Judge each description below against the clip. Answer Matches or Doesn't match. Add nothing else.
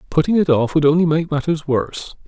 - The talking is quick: Matches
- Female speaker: Doesn't match